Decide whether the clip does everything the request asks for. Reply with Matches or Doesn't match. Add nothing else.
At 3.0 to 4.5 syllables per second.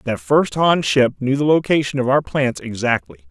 Doesn't match